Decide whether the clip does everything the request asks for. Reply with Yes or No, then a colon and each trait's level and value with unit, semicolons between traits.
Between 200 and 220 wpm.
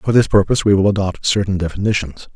Yes: fast, 205 wpm